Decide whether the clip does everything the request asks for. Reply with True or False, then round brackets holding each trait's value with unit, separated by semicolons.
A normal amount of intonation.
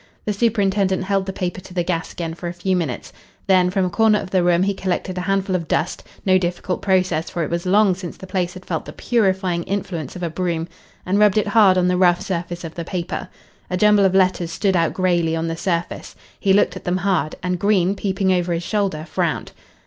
False (2.0 semitones)